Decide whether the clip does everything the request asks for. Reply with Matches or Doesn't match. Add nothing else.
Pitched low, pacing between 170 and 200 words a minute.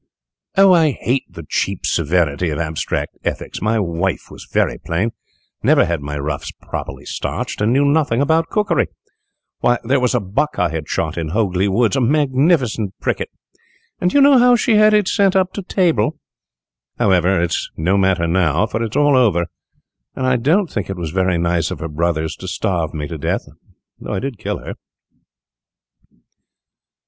Matches